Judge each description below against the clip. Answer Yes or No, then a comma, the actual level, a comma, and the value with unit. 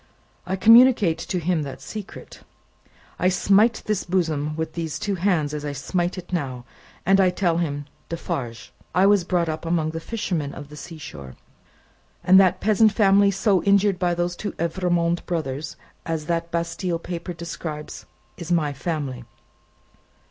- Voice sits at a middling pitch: Yes, medium, 170 Hz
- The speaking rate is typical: Yes, average, 160 wpm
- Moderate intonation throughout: Yes, average, 3.3 semitones